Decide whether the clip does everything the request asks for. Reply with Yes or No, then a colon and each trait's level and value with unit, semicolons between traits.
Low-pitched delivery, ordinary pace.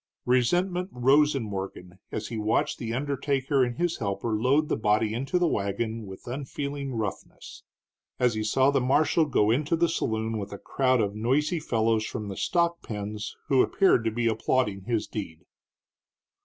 Yes: low, 120 Hz; average, 170 wpm